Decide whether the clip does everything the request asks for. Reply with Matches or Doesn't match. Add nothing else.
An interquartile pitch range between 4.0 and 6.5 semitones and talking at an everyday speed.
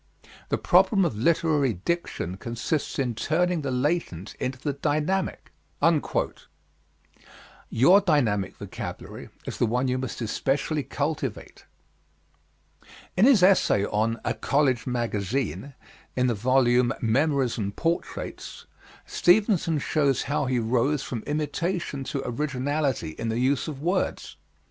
Doesn't match